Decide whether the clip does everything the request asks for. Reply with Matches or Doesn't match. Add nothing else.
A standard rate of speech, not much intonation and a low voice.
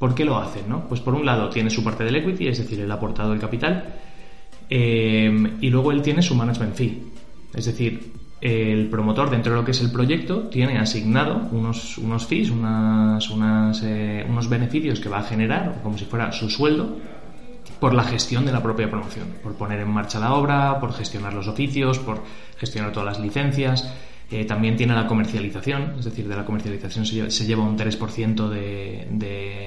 Doesn't match